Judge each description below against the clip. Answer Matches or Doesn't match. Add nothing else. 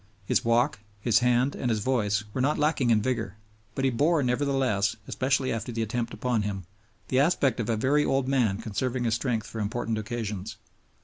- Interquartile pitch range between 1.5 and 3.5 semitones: Matches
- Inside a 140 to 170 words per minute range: Doesn't match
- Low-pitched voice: Matches